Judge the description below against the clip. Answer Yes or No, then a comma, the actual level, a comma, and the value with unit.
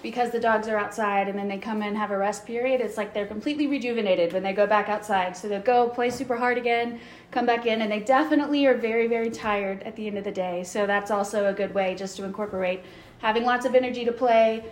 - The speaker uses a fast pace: Yes, fast, 255 wpm